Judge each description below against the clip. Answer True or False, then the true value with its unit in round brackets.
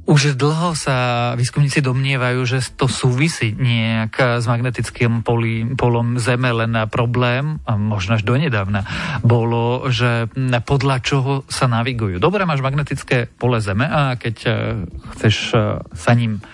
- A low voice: True (125 Hz)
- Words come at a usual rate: True (130 wpm)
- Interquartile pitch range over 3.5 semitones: False (2.6 semitones)